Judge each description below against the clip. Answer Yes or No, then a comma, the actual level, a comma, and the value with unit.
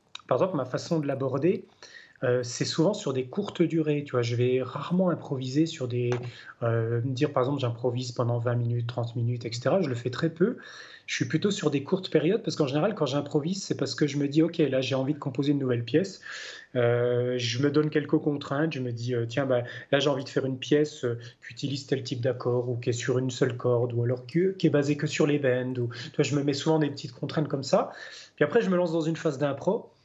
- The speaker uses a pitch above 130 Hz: Yes, medium, 140 Hz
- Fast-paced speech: Yes, fast, 255 wpm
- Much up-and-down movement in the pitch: No, average, 4.0 semitones